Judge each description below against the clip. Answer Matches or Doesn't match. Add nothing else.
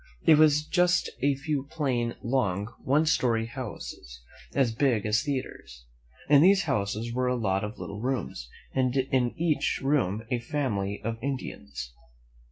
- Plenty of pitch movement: Doesn't match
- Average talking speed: Matches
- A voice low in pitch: Matches